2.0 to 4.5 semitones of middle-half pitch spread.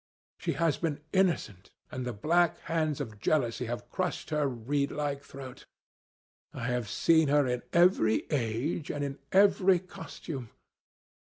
No: average, 5.0 semitones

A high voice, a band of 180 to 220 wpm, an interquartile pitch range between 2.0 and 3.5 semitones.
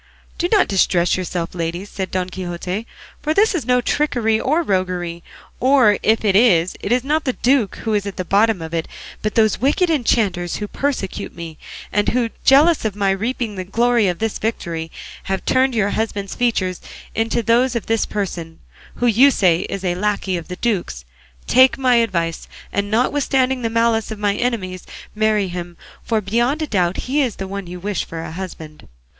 No: high, 210 Hz; average, 190 wpm; average, 4.9 semitones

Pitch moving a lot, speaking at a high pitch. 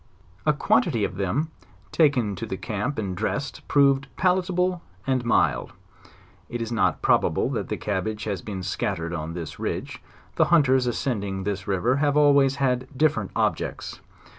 No: wide, 6.2 semitones; low, 120 Hz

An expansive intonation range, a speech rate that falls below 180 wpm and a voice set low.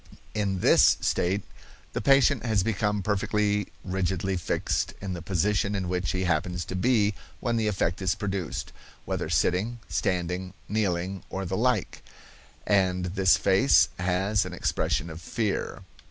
No: narrow, 2.5 semitones; average, 145 wpm; very low, 95 Hz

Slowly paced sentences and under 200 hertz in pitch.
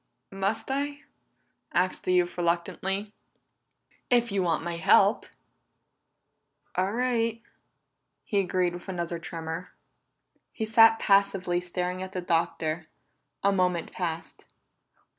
Yes: slow, 110 wpm; medium, 185 Hz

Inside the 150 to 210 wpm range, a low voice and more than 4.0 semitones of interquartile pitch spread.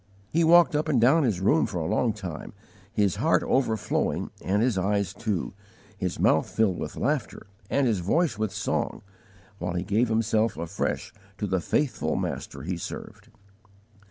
Yes: average, 165 wpm; low, 105 Hz; average, 4.8 semitones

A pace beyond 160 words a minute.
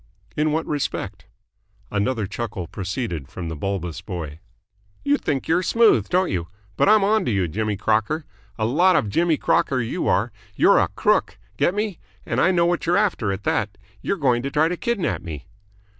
Yes: average, 185 wpm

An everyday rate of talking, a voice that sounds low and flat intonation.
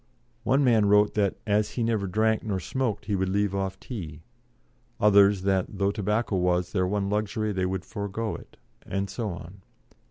Yes: average, 180 wpm; low, 100 Hz; narrow, 2.1 semitones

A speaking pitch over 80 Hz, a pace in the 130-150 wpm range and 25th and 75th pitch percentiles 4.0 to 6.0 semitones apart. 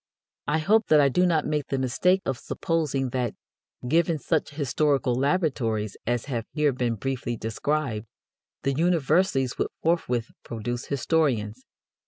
Yes: low, 135 Hz; average, 140 wpm; average, 4.6 semitones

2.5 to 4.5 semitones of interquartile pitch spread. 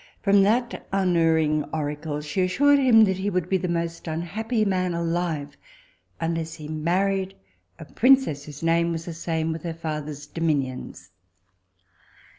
Yes: average, 3.4 semitones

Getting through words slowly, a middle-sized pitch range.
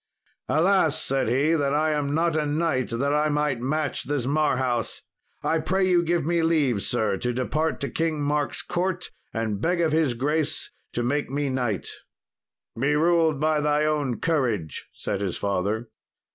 No: average, 170 wpm; average, 4.1 semitones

